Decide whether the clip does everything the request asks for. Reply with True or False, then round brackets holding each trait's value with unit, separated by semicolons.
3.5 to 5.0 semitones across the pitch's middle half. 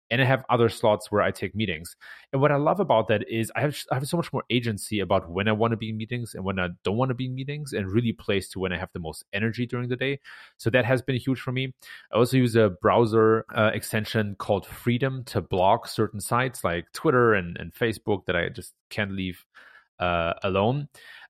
True (4.2 semitones)